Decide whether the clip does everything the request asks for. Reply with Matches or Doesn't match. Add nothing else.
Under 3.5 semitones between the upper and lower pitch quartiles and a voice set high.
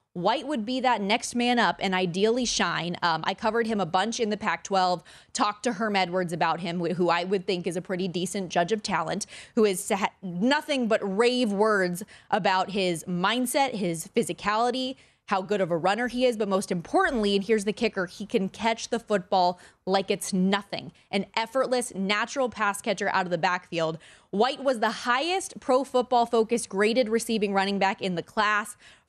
Doesn't match